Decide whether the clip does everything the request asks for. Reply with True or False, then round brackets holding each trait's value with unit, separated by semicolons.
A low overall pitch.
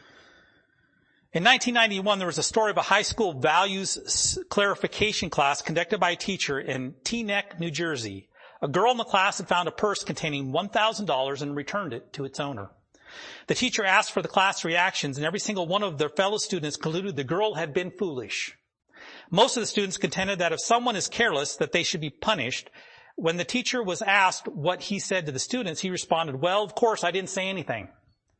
False (190 Hz)